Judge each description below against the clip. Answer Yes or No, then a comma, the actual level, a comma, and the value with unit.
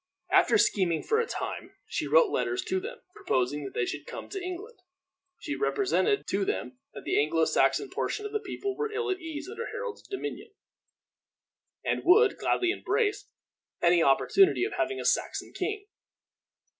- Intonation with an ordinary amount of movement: No, wide, 6.6 semitones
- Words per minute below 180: Yes, average, 170 wpm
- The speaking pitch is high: Yes, very high, 390 Hz